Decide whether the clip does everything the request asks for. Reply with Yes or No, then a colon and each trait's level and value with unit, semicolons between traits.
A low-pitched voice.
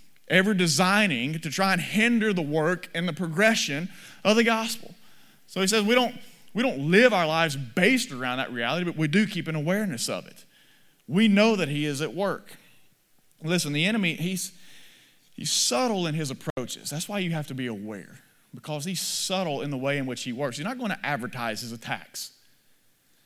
No: medium, 175 Hz